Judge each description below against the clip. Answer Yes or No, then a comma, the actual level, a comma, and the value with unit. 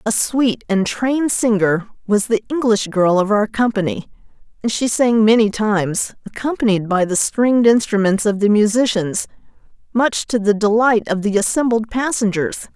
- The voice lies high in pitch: Yes, high, 220 Hz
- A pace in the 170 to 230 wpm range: No, average, 155 wpm